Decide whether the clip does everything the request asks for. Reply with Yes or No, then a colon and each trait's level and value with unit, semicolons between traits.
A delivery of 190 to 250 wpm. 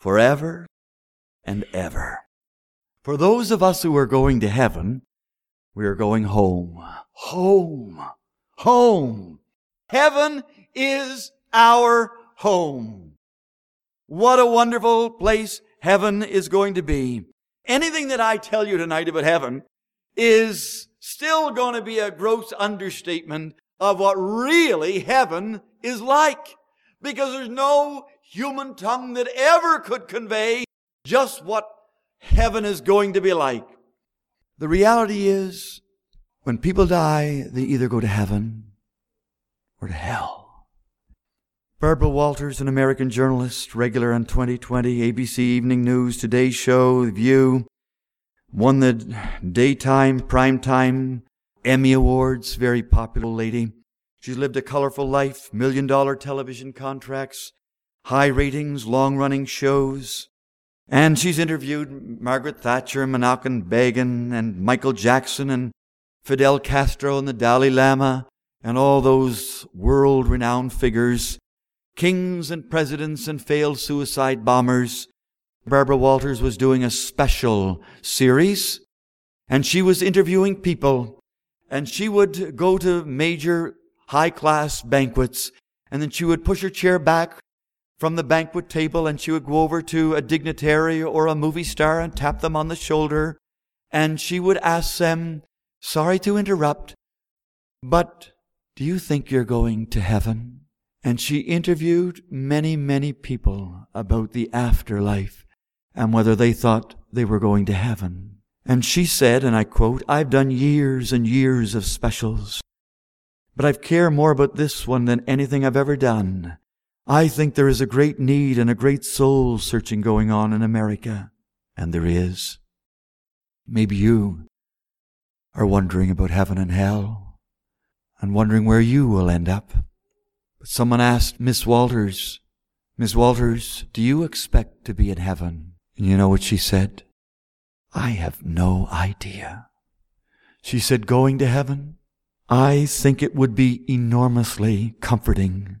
No: slow, 135 wpm